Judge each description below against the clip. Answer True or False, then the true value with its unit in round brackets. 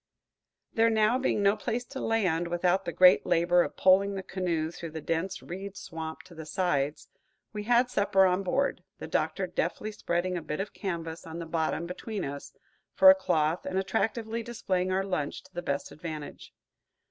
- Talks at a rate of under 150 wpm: False (185 wpm)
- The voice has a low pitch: False (185 Hz)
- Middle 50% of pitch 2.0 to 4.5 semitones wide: True (3.8 semitones)